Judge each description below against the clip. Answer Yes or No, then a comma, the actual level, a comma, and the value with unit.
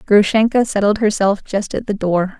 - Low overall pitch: No, high, 205 Hz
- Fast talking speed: No, average, 175 wpm